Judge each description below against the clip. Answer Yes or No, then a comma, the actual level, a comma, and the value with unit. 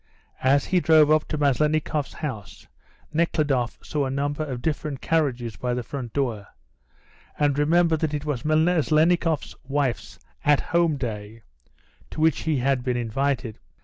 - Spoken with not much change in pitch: No, average, 3.6 semitones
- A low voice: No, medium, 145 Hz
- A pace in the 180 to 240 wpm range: No, average, 145 wpm